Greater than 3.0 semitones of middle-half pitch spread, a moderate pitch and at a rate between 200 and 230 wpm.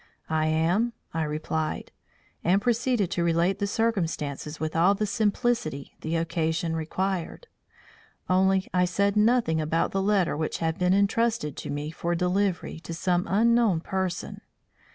No: average, 3.8 semitones; medium, 180 Hz; average, 145 wpm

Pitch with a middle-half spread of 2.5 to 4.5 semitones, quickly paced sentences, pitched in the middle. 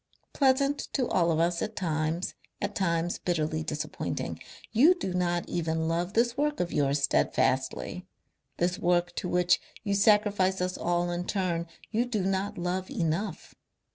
No: average, 3.4 semitones; average, 155 wpm; medium, 180 Hz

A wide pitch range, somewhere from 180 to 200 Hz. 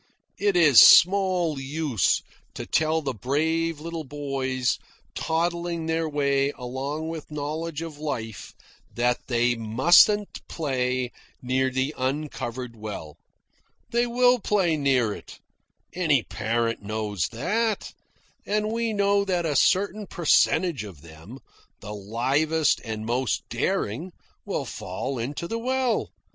No: wide, 5.7 semitones; medium, 145 Hz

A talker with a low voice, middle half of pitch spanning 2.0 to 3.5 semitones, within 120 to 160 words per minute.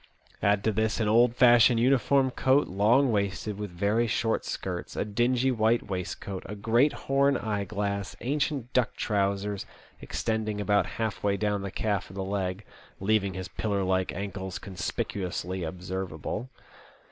Yes: low, 105 Hz; average, 3.2 semitones; average, 155 wpm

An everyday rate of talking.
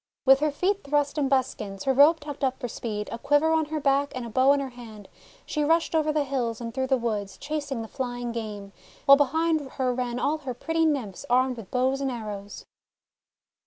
No: fast, 215 wpm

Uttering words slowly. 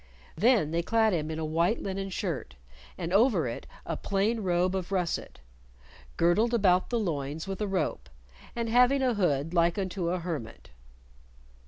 No: average, 165 wpm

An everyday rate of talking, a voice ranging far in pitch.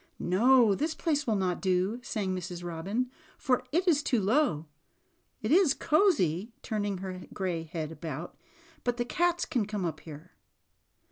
Yes: average, 160 wpm; wide, 6.4 semitones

